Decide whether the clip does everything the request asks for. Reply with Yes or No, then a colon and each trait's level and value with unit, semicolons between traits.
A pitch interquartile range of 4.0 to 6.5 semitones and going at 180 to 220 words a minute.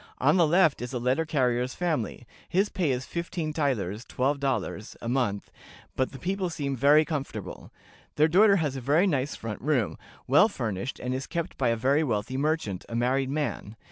Yes: average, 4.4 semitones; average, 190 wpm